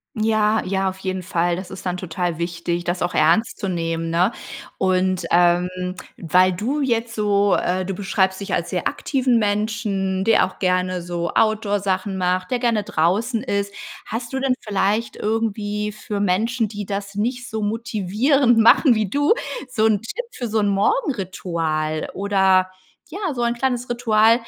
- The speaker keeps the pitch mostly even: No, average, 3.6 semitones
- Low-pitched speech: No, high, 200 Hz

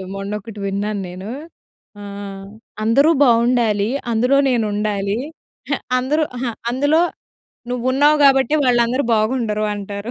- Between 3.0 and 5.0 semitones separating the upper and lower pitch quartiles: Yes, average, 4.1 semitones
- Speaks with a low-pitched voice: No, high, 225 Hz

